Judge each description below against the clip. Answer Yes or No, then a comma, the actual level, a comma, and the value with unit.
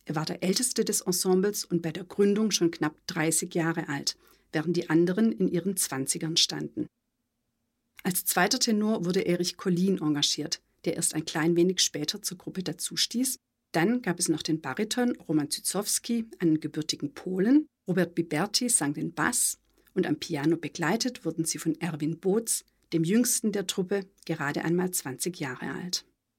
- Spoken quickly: No, average, 165 wpm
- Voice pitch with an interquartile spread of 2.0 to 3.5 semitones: No, average, 3.9 semitones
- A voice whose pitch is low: No, medium, 175 Hz